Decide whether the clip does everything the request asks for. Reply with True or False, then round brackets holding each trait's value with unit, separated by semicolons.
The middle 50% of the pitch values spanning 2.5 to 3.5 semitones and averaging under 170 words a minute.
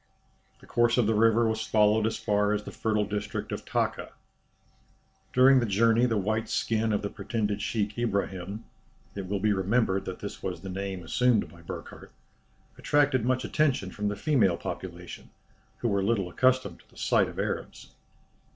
False (2.9 semitones; 175 wpm)